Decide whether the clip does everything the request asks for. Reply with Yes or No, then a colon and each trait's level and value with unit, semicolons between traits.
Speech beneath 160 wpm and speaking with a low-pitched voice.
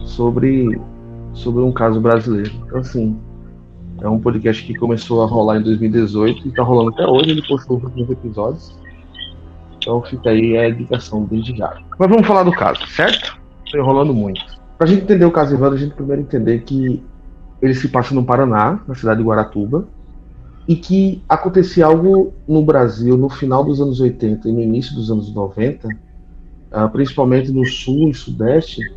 No: average, 175 wpm; low, 120 Hz